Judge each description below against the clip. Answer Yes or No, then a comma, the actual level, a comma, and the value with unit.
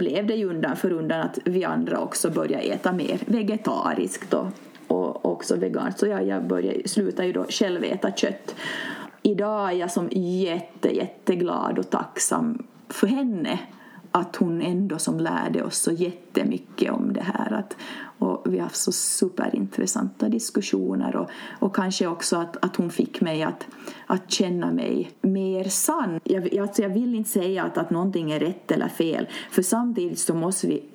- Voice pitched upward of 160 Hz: Yes, high, 190 Hz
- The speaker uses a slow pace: No, average, 170 wpm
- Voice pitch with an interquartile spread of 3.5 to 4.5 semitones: Yes, average, 3.9 semitones